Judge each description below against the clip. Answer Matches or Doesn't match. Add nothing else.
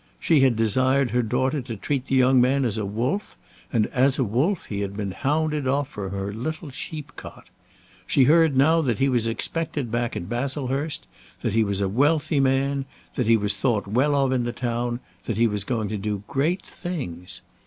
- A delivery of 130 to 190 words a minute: Doesn't match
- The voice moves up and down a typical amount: Matches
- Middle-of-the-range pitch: Doesn't match